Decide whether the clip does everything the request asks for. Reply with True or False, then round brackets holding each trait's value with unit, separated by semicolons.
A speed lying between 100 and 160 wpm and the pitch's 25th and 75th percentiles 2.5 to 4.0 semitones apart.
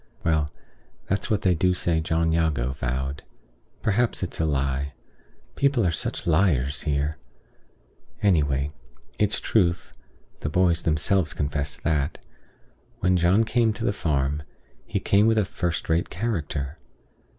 False (135 wpm; 4.8 semitones)